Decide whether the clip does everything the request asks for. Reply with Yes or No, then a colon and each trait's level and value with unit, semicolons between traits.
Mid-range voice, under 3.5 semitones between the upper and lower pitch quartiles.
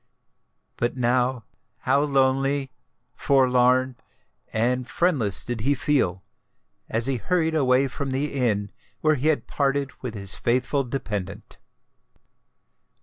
No: low, 130 Hz; narrow, 2.6 semitones